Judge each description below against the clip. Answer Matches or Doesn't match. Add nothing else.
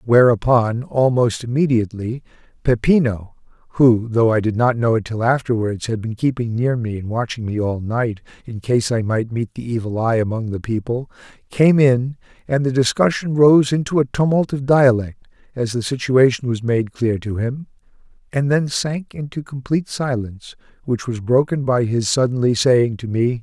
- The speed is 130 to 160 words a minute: Doesn't match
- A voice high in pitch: Doesn't match